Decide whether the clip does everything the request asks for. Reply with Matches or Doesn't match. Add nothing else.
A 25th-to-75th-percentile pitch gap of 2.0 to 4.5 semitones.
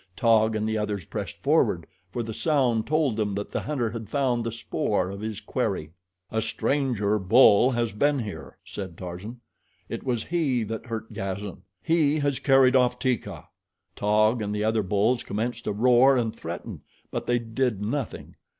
Matches